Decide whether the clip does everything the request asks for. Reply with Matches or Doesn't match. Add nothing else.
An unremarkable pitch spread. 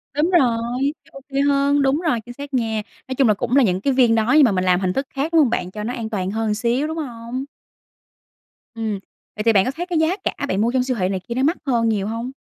Matches